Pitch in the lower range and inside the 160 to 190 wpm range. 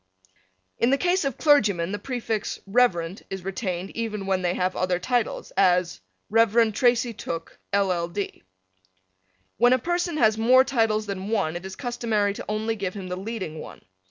No: high, 210 Hz; average, 170 wpm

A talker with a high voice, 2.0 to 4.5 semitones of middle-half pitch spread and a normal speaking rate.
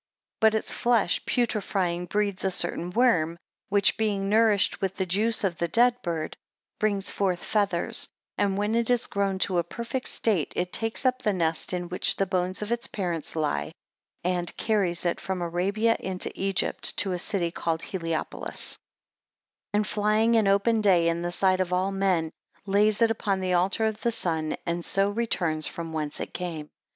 Yes: high, 195 Hz; average, 3.5 semitones; average, 185 wpm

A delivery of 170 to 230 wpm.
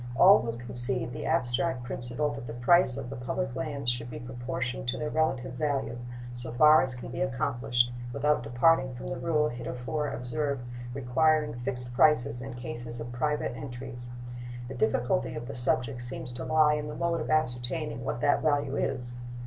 Yes: average, 180 wpm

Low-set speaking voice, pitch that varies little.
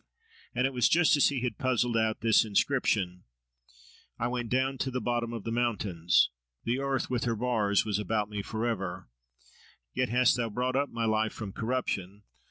No: low, 115 Hz; average, 3.1 semitones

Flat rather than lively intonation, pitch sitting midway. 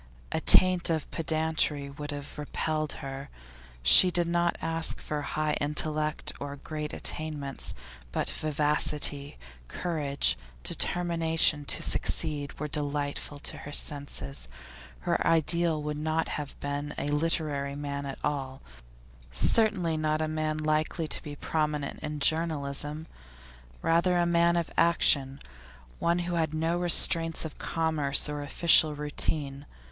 Yes: narrow, 2.2 semitones; medium, 150 Hz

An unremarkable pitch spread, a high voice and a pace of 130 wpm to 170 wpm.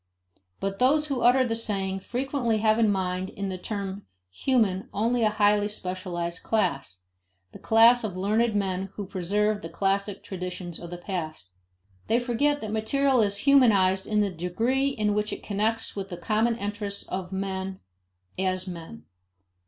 Yes: average, 3.2 semitones; high, 205 Hz; average, 160 wpm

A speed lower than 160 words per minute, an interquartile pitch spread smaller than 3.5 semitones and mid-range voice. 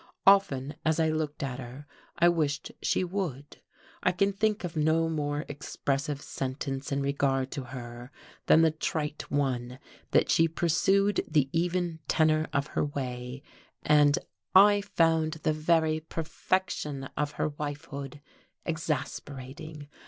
Yes: slow, 135 wpm; average, 2.9 semitones; medium, 150 Hz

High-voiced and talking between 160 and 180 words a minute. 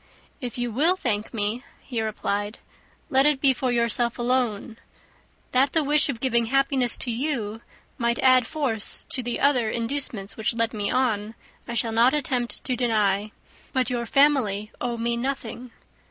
Yes: high, 240 Hz; average, 165 wpm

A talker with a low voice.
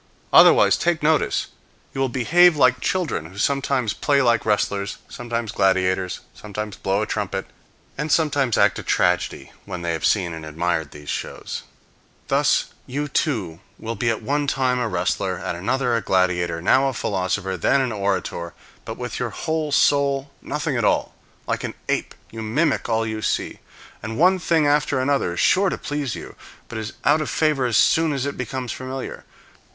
Yes: low, 120 Hz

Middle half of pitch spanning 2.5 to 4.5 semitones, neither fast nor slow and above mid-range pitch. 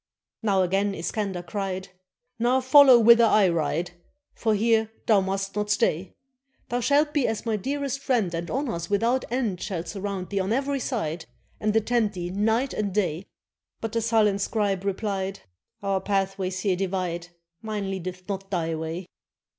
Yes: average, 3.5 semitones; average, 160 wpm; high, 200 Hz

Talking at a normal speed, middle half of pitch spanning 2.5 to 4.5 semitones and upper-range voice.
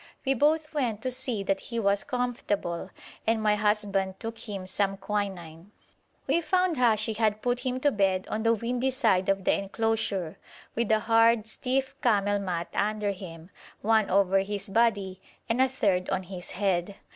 Yes: average, 170 wpm; average, 3.4 semitones; high, 210 Hz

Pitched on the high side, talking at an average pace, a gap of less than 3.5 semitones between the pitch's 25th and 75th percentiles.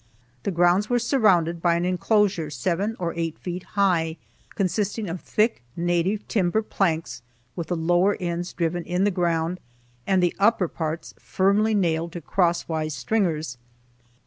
No: medium, 175 Hz; average, 150 wpm; average, 3.0 semitones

